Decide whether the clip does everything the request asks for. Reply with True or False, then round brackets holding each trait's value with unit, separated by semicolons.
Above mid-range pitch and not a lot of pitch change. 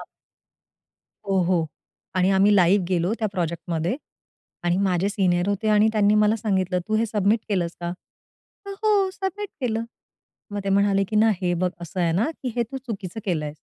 False (200 Hz; 3.6 semitones)